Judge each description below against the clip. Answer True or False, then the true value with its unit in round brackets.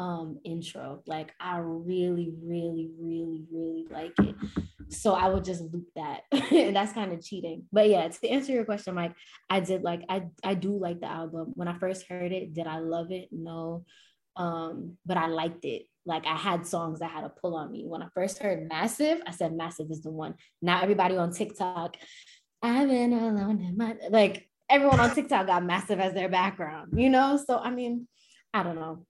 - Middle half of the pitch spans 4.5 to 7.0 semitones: False (3.8 semitones)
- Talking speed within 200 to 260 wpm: True (205 wpm)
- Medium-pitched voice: True (180 Hz)